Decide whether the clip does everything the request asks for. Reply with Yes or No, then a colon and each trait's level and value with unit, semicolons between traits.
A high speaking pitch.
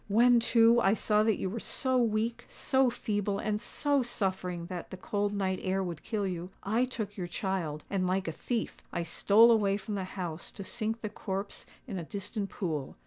Yes: high, 205 Hz